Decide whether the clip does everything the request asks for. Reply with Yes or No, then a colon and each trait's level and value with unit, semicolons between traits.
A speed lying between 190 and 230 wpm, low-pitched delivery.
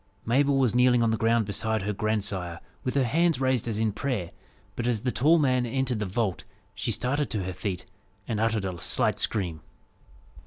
Yes: average, 195 wpm; low, 115 Hz